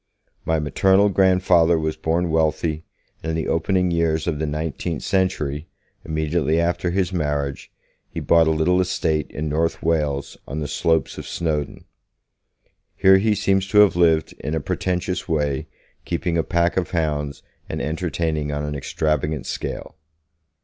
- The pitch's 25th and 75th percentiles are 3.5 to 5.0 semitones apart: No, narrow, 2.5 semitones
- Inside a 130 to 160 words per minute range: Yes, average, 155 wpm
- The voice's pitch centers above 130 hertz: No, very low, 80 Hz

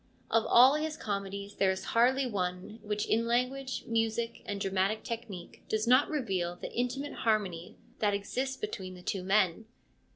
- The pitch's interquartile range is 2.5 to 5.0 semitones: Yes, average, 4.2 semitones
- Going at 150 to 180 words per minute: Yes, average, 160 wpm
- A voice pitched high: Yes, high, 220 Hz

